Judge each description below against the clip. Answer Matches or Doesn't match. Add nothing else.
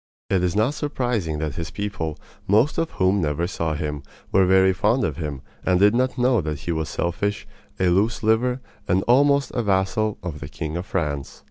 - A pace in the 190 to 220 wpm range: Matches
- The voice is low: Matches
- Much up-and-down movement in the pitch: Matches